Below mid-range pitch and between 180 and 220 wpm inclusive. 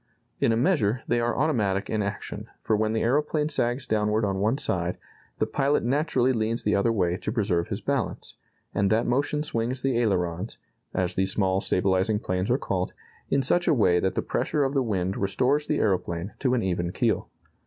Yes: low, 110 Hz; average, 195 wpm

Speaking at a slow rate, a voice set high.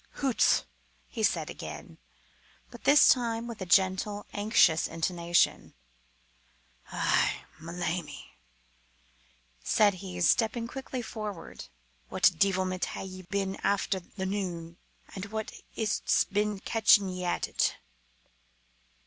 Yes: slow, 115 wpm; high, 195 Hz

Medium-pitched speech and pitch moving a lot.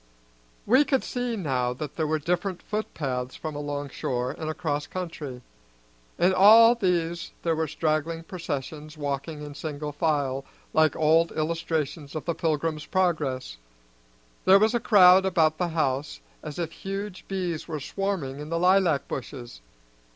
No: medium, 160 Hz; average, 3.8 semitones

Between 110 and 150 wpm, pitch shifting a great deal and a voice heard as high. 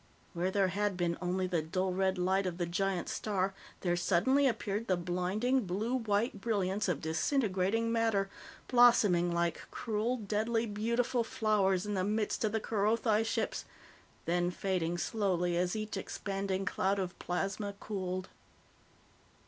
No: average, 145 wpm; average, 3.2 semitones; high, 195 Hz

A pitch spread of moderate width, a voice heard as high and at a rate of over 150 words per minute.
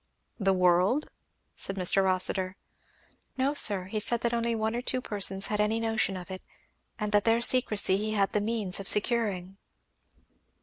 Yes: average, 3.1 semitones; high, 210 Hz; average, 170 wpm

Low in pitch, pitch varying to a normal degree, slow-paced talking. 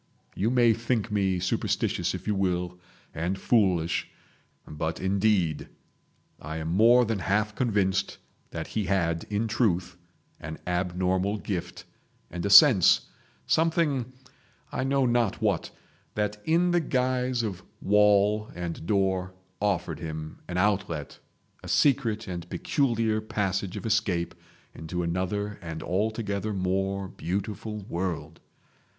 Yes: low, 100 Hz; average, 3.8 semitones; slow, 120 wpm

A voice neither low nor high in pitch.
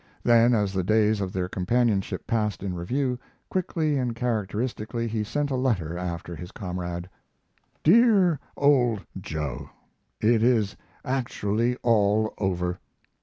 No: low, 110 Hz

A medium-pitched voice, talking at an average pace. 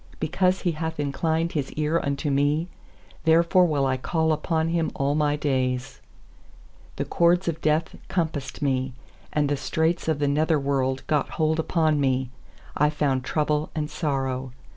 Yes: medium, 150 Hz; average, 160 wpm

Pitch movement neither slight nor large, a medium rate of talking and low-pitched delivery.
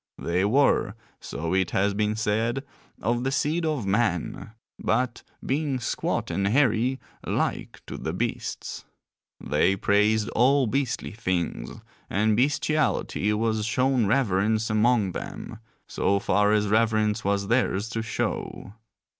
No: average, 3.7 semitones; slow, 130 wpm; low, 110 Hz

